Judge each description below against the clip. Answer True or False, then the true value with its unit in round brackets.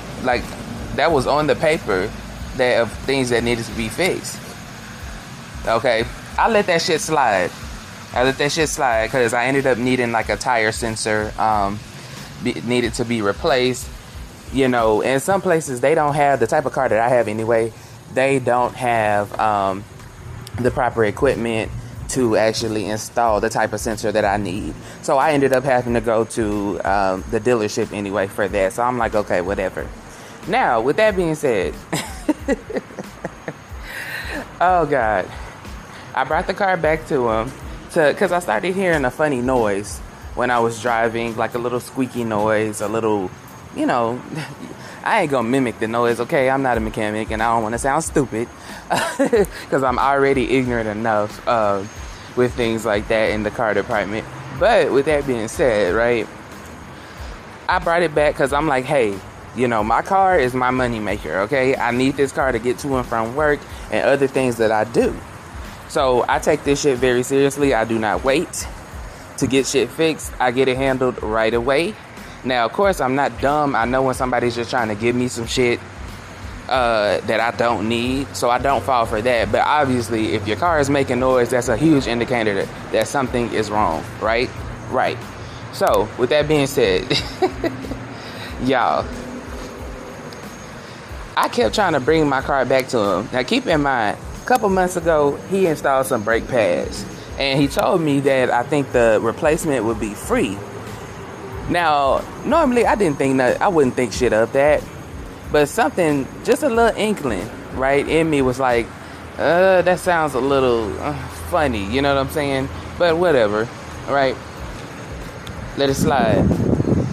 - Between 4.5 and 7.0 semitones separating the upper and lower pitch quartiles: False (3.9 semitones)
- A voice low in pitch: True (125 Hz)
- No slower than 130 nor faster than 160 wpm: False (180 wpm)